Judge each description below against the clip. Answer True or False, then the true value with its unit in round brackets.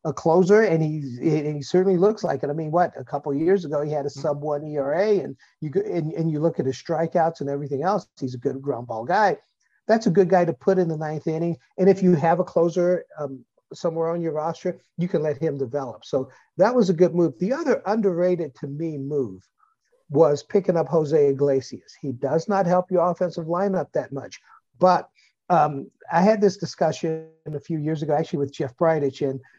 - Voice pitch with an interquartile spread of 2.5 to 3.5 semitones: False (3.9 semitones)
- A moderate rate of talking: False (220 wpm)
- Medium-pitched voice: True (160 Hz)